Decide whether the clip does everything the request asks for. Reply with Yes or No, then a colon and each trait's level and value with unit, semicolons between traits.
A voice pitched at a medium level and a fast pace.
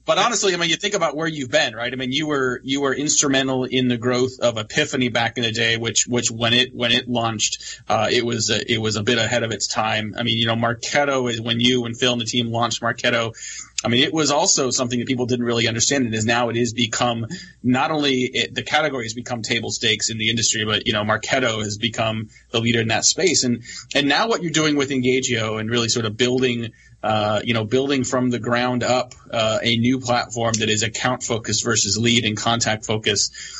No: low, 120 Hz; fast, 240 wpm